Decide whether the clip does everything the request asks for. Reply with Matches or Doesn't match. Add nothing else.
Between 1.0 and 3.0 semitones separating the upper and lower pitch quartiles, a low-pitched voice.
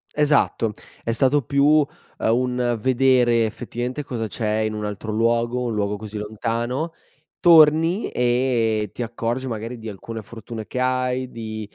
Matches